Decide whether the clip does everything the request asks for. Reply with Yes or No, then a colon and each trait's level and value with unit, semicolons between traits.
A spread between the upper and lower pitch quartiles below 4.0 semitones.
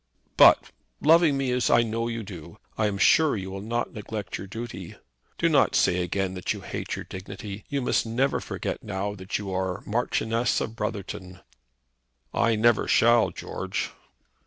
Yes: average, 3.5 semitones